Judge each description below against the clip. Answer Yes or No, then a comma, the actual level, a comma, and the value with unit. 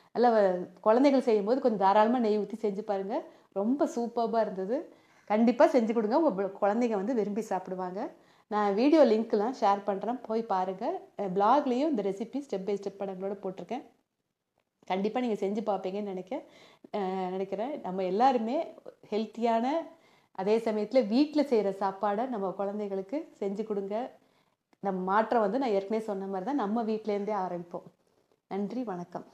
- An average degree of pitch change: Yes, average, 3.7 semitones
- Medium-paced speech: No, fast, 135 wpm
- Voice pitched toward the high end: Yes, high, 215 Hz